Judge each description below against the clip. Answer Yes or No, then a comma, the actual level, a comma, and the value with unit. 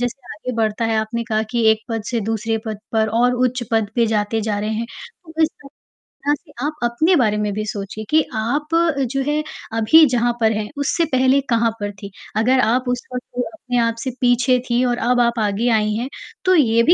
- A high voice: Yes, high, 235 Hz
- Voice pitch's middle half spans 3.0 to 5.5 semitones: No, narrow, 2.6 semitones